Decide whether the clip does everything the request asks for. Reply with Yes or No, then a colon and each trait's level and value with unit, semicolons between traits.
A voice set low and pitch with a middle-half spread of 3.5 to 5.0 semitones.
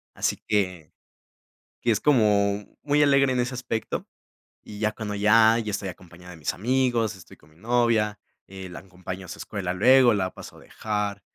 Yes: low, 105 Hz; average, 4.0 semitones